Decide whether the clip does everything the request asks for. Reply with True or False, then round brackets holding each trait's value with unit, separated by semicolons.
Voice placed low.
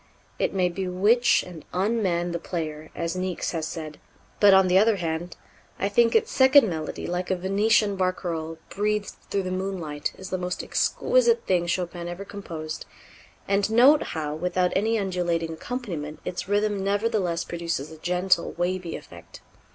False (185 Hz)